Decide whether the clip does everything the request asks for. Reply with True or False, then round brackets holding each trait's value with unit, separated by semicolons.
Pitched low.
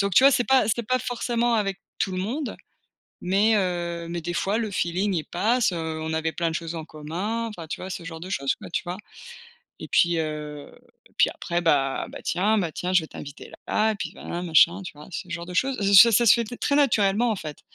False (180 Hz)